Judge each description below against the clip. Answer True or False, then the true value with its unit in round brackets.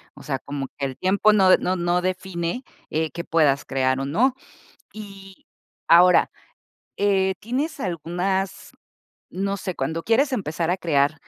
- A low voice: False (180 Hz)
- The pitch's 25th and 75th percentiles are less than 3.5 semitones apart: False (3.8 semitones)